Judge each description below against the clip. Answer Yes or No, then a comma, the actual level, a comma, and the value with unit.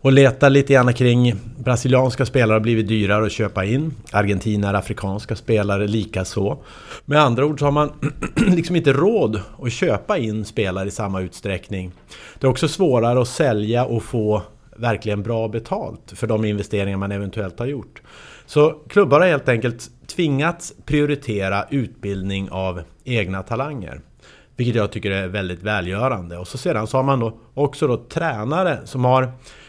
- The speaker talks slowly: No, average, 160 wpm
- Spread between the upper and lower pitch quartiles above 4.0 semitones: Yes, average, 4.8 semitones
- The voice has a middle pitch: No, low, 115 Hz